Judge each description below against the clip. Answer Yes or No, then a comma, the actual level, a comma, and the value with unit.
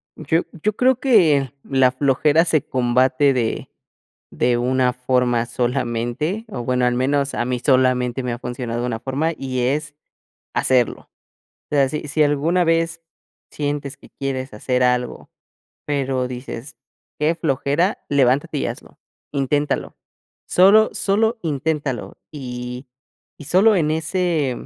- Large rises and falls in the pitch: No, average, 3.8 semitones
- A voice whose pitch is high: No, low, 135 Hz